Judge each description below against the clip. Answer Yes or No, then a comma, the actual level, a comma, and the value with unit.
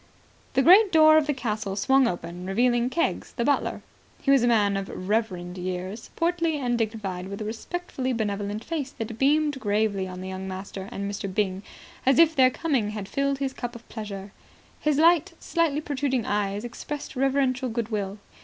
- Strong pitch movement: Yes, wide, 5.7 semitones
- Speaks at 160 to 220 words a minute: Yes, average, 180 wpm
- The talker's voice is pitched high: Yes, high, 235 Hz